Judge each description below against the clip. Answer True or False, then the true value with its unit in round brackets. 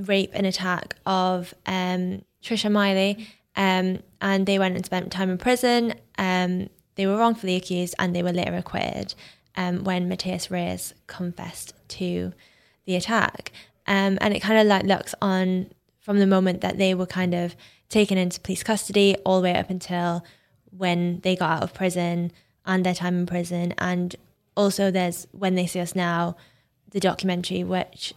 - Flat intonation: True (1.6 semitones)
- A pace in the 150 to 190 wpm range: True (175 wpm)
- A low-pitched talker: False (185 Hz)